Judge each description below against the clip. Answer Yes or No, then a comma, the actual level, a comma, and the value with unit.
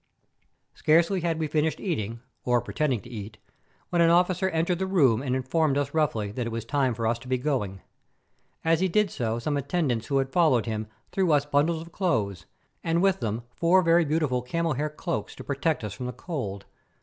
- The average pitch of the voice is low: No, medium, 145 Hz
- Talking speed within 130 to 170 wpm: No, fast, 205 wpm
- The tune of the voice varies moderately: No, wide, 5.8 semitones